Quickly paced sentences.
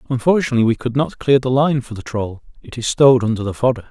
Yes: fast, 230 wpm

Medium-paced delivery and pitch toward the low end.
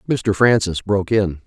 Yes: average, 165 wpm; low, 100 Hz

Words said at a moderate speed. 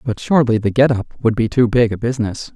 No: fast, 260 wpm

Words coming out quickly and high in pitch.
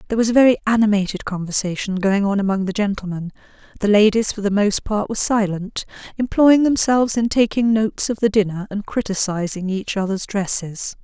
No: average, 175 wpm; high, 205 Hz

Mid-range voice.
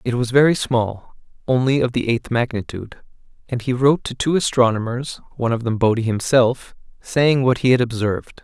No: low, 125 Hz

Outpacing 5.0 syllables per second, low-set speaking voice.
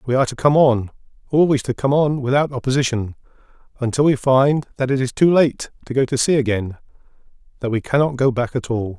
Yes: 5.9 syllables/s; low, 130 Hz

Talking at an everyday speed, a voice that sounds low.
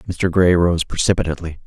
Yes: average, 145 wpm; very low, 85 Hz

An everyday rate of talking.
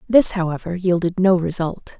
Yes: average, 150 wpm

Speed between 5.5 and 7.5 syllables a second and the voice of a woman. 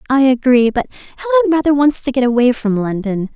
Yes: 6.3 syllables/s; female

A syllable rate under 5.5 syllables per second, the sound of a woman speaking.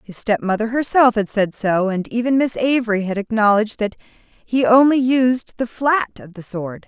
Yes: 4.7 syllables/s; female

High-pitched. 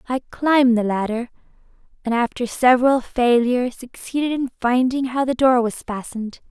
Yes: high, 245 Hz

